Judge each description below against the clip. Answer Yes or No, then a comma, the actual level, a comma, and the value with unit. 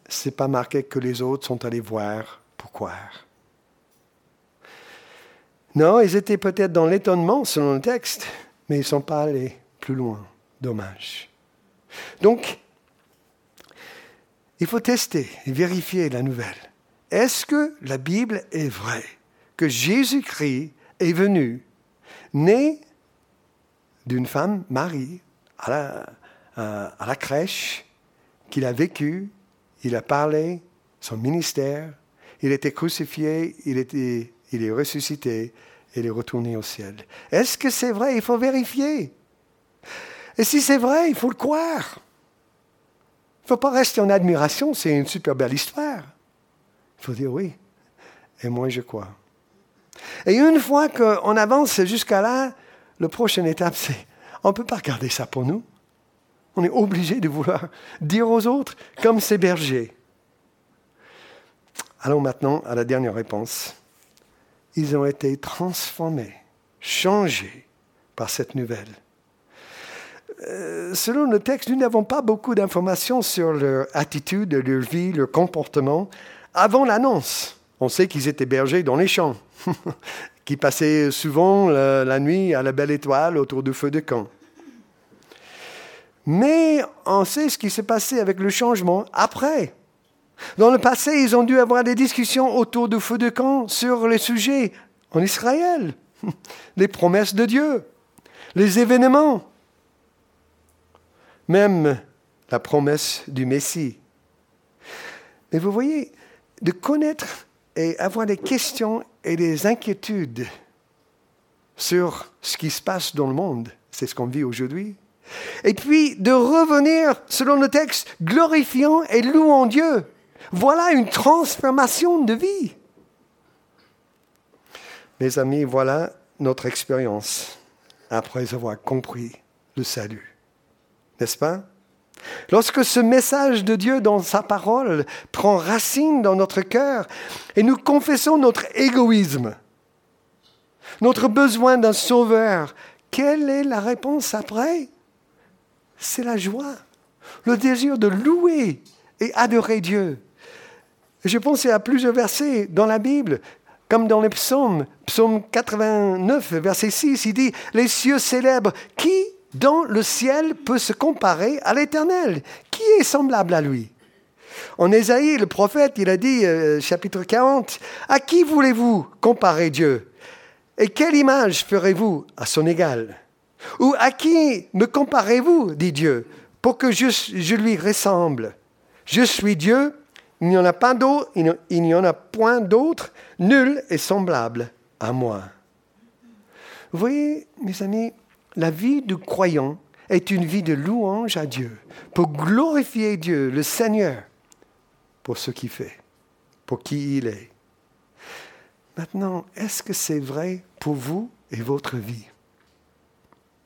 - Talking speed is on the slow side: Yes, slow, 135 wpm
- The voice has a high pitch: Yes, high, 195 Hz